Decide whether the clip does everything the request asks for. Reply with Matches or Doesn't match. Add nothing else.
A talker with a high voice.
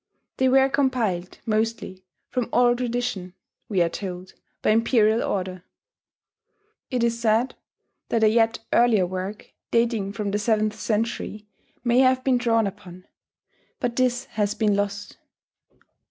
Matches